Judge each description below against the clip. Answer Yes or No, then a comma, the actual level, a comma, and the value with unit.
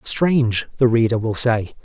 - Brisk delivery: No, average, 165 wpm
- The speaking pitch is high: No, low, 120 Hz